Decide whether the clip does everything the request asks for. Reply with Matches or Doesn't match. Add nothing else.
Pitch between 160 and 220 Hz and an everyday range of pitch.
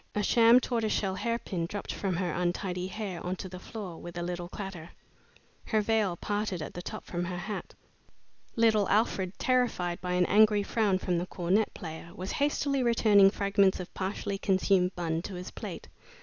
Matches